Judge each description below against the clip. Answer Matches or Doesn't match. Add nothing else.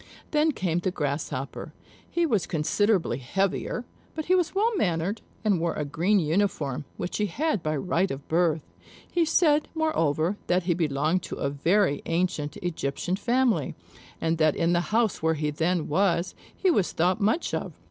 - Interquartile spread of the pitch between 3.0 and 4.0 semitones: Doesn't match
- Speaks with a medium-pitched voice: Matches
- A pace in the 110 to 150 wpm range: Doesn't match